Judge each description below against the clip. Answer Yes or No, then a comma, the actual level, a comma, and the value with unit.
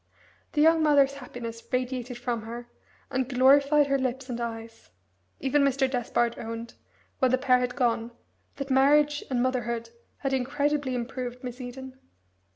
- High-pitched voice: Yes, very high, 255 Hz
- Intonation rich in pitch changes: No, narrow, 2.4 semitones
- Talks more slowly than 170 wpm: Yes, average, 150 wpm